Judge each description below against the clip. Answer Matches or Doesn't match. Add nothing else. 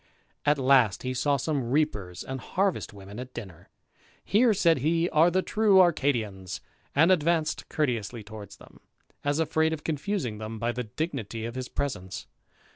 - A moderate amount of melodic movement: Doesn't match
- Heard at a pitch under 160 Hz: Matches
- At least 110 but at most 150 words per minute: Doesn't match